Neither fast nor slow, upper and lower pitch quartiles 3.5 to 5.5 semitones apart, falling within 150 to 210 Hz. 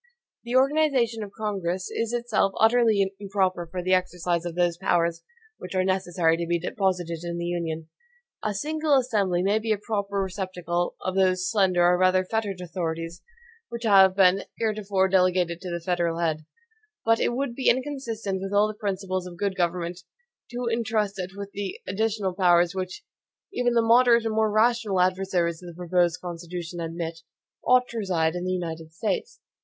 Yes: average, 175 wpm; average, 3.8 semitones; high, 190 Hz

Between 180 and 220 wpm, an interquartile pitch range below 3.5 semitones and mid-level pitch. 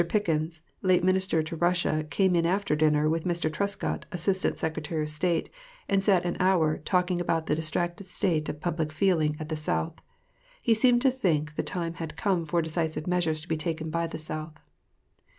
Yes: average, 185 wpm; narrow, 2.6 semitones; medium, 165 Hz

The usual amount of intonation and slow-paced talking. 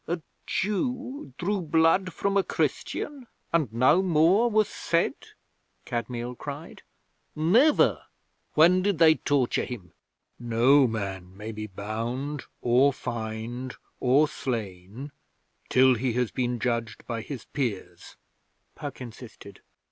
No: wide, 6.4 semitones; slow, 120 wpm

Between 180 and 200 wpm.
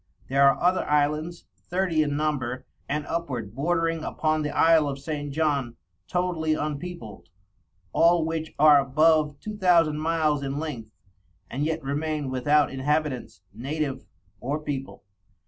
No: slow, 135 wpm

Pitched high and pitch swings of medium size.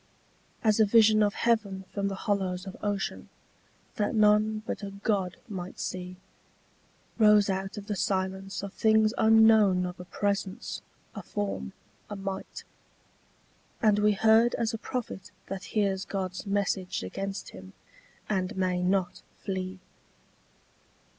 No: high, 200 Hz; narrow, 2.1 semitones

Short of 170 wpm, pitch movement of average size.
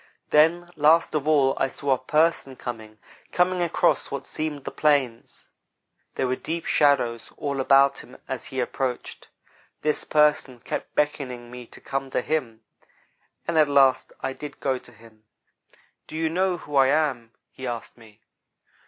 Yes: average, 160 wpm; average, 3.4 semitones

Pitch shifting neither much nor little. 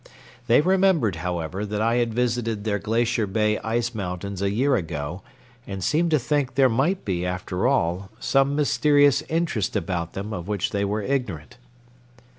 No: wide, 5.8 semitones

